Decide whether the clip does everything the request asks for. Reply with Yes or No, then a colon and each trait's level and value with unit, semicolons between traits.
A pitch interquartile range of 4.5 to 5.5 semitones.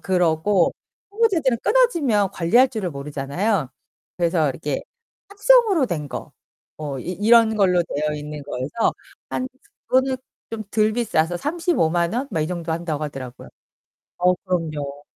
No: wide, 7.5 semitones